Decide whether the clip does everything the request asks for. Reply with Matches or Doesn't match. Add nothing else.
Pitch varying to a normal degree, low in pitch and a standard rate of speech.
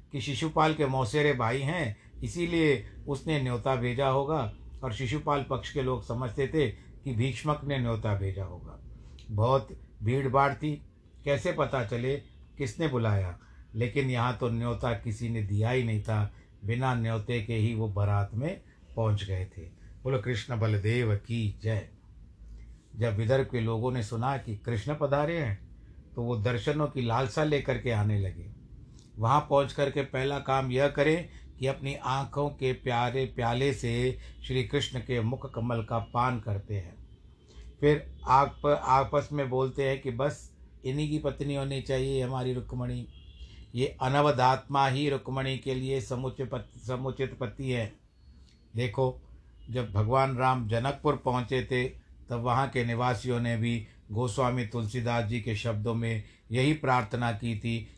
Matches